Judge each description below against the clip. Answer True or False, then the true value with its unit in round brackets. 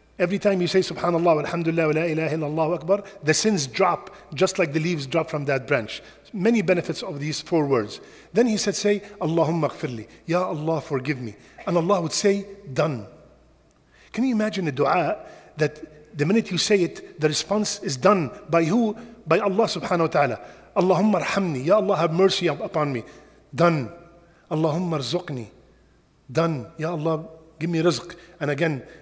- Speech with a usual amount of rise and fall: True (3.7 semitones)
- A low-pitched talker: False (165 Hz)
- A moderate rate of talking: True (180 wpm)